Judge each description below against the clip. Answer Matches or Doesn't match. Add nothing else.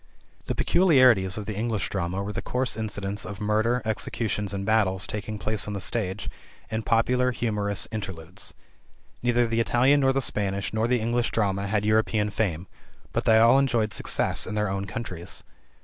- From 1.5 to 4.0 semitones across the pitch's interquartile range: Matches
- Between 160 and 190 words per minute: Matches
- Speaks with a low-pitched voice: Matches